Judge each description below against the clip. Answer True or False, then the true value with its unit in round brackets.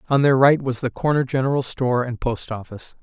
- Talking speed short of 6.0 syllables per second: False (6.1 syllables/s)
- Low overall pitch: True (130 Hz)